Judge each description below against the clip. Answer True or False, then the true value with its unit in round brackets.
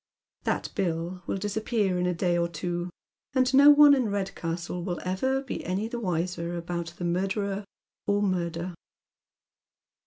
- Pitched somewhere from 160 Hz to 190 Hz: True (185 Hz)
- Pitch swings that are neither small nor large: True (3.2 semitones)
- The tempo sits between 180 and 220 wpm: False (155 wpm)